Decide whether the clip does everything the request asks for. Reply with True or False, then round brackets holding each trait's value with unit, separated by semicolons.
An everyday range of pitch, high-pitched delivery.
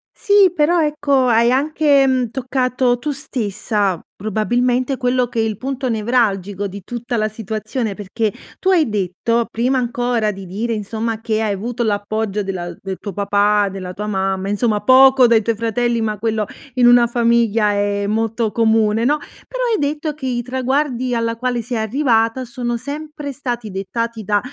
True (3.3 semitones; 230 Hz)